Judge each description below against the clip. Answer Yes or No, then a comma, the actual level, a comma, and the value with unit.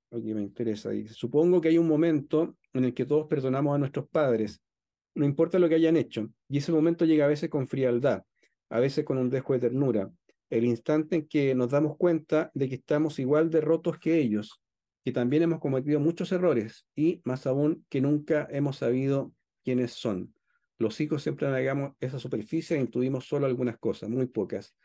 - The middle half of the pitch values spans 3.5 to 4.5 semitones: Yes, average, 3.8 semitones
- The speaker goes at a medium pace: No, fast, 195 wpm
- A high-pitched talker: No, medium, 140 Hz